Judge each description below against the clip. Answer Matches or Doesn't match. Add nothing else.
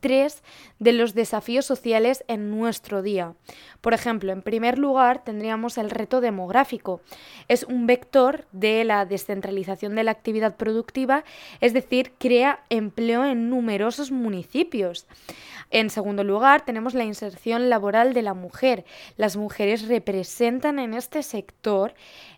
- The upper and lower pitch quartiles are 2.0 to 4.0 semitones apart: Matches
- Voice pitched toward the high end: Matches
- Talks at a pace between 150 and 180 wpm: Doesn't match